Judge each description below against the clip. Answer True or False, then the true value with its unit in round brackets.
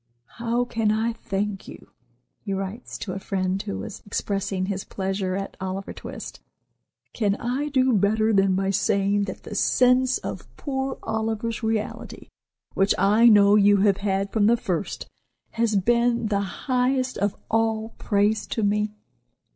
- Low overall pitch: False (210 Hz)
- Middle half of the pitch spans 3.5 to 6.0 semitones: False (2.7 semitones)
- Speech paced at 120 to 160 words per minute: True (155 wpm)